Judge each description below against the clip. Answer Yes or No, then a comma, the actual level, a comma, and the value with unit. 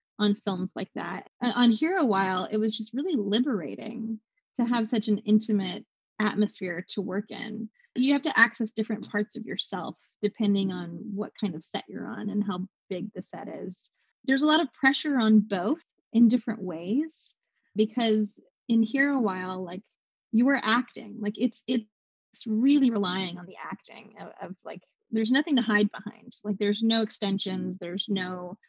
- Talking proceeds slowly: No, average, 175 wpm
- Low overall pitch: No, high, 215 Hz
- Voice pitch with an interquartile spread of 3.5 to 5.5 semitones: No, average, 3.0 semitones